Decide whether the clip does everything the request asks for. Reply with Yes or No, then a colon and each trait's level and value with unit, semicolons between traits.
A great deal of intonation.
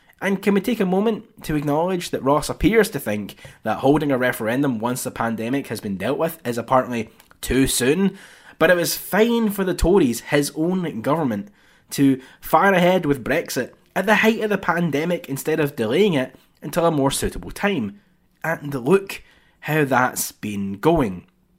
Yes: wide, 6.4 semitones